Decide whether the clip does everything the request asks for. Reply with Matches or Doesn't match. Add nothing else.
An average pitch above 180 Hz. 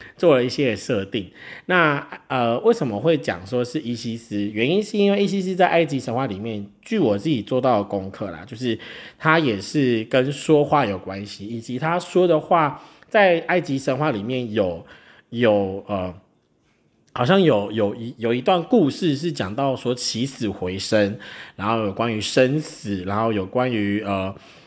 Doesn't match